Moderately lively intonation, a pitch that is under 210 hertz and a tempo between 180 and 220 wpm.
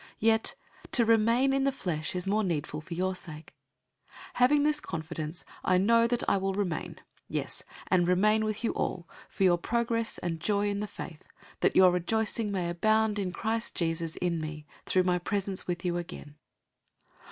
Yes: average, 4.3 semitones; high, 190 Hz; average, 185 wpm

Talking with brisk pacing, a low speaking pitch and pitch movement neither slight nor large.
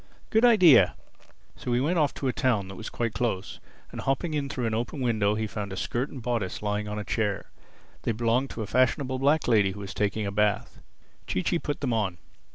Yes: fast, 225 wpm; low, 115 Hz; average, 4.3 semitones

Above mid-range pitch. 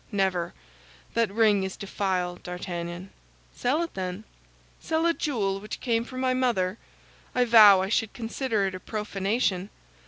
Yes: high, 205 Hz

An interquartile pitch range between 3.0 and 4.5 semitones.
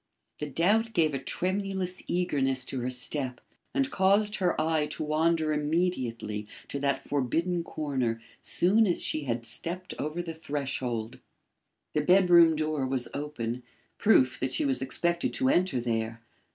No: average, 5.3 semitones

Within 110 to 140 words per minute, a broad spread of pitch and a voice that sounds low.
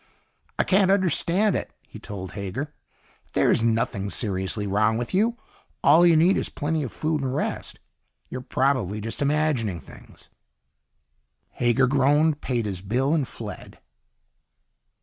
Yes: slow, 135 wpm; wide, 6.5 semitones; low, 130 Hz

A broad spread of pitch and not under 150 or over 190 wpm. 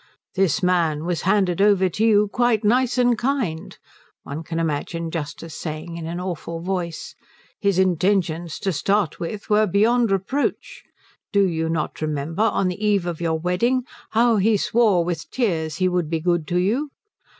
No: average, 4.1 semitones; average, 170 wpm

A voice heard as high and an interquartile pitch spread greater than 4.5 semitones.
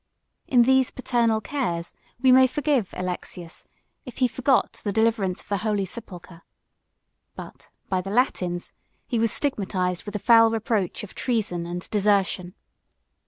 Yes: high, 210 Hz; average, 4.9 semitones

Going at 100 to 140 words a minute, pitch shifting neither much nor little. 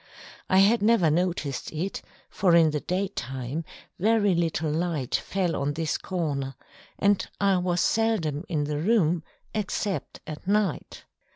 Yes: slow, 135 wpm; average, 4.5 semitones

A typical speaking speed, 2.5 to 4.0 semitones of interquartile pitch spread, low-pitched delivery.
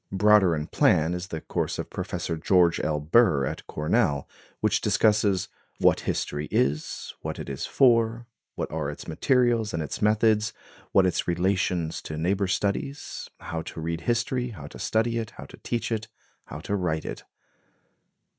No: average, 165 wpm; wide, 5.6 semitones; very low, 95 Hz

